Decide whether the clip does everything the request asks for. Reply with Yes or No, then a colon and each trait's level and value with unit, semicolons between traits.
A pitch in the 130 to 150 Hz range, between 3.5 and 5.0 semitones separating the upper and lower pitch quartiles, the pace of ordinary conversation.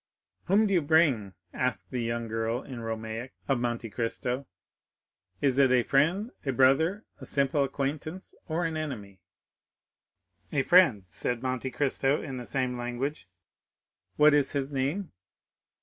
Yes: low, 135 Hz; average, 3.8 semitones; average, 145 wpm